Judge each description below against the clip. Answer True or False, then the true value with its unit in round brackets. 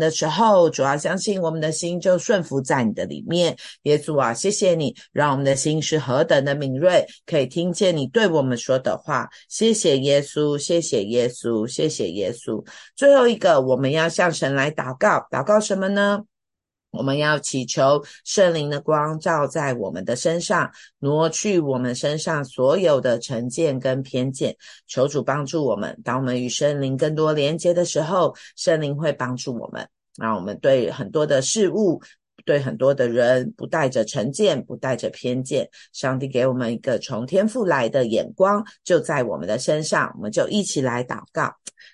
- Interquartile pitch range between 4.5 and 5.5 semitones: True (4.8 semitones)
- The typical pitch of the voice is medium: True (150 Hz)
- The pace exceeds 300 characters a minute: False (265 characters per minute)